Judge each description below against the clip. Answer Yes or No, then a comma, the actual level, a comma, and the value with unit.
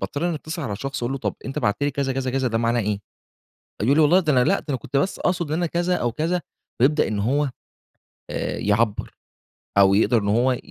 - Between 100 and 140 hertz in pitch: Yes, low, 135 Hz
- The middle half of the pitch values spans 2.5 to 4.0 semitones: No, average, 5.0 semitones